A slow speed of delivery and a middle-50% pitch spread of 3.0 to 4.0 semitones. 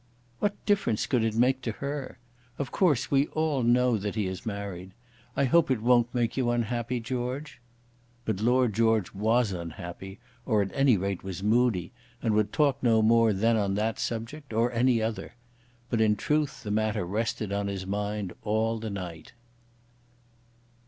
No: average, 170 wpm; average, 3.5 semitones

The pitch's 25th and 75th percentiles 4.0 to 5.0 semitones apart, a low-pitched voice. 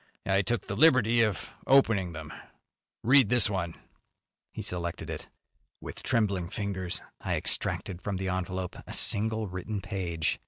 No: average, 3.4 semitones; low, 100 Hz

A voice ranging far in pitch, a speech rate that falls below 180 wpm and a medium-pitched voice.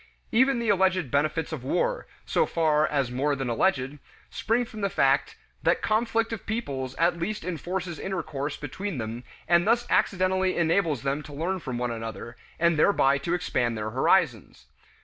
Yes: wide, 6.0 semitones; average, 170 wpm; medium, 165 Hz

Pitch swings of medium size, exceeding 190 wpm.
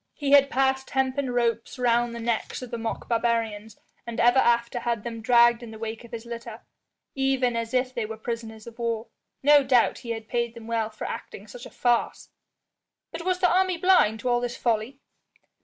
No: narrow, 2.0 semitones; fast, 205 wpm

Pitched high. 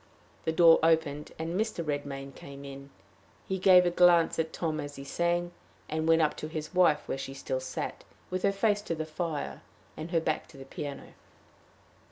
No: medium, 160 Hz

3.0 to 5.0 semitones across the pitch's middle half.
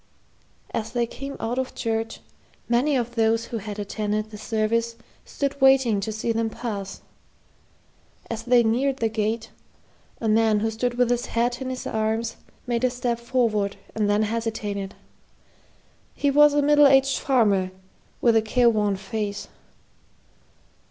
No: narrow, 2.4 semitones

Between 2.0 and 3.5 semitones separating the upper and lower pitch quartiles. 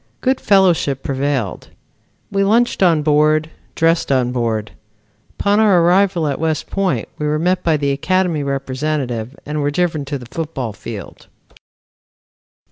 No: average, 4.5 semitones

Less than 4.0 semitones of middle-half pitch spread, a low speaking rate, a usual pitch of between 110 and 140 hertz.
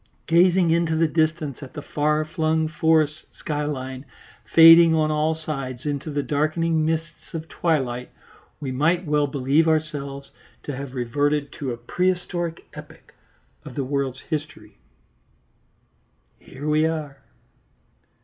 No: narrow, 2.4 semitones; slow, 130 wpm; medium, 155 Hz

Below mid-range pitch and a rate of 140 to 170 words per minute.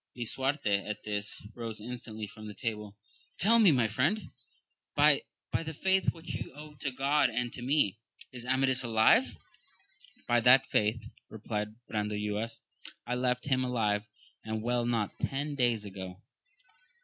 Yes: low, 120 Hz; average, 150 wpm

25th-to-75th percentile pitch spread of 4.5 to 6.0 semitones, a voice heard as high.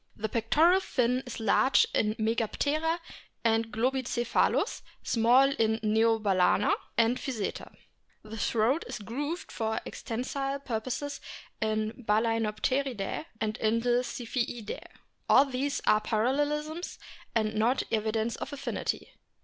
No: average, 3.5 semitones; high, 230 Hz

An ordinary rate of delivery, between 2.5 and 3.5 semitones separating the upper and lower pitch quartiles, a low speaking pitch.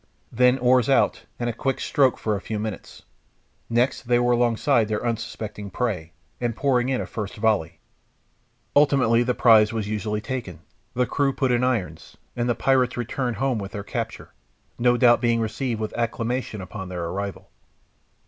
Yes: average, 170 wpm; average, 2.8 semitones; low, 120 Hz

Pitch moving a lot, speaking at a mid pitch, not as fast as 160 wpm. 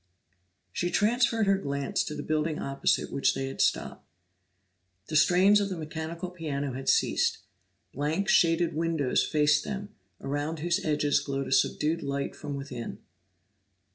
No: average, 3.9 semitones; medium, 155 Hz; average, 145 wpm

